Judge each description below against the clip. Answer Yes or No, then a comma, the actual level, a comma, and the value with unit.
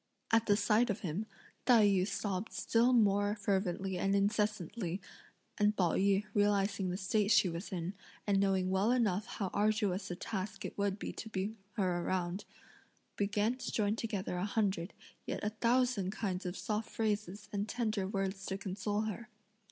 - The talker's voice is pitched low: No, high, 200 Hz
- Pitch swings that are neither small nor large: No, narrow, 2.0 semitones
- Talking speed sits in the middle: Yes, average, 170 wpm